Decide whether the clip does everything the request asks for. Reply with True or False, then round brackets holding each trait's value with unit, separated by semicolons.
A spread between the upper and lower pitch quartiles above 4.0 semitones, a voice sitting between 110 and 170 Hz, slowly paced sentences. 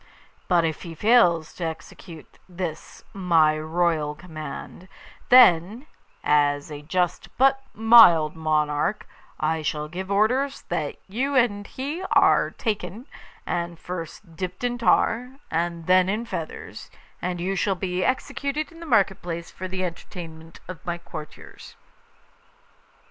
False (5.2 semitones; 180 Hz; 130 wpm)